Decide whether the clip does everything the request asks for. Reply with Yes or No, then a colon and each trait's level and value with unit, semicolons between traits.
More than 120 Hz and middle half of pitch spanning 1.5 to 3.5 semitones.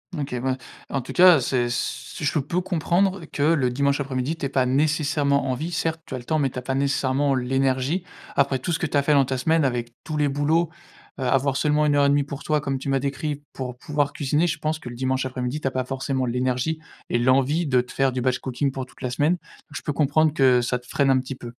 Yes: medium, 140 Hz; average, 2.7 semitones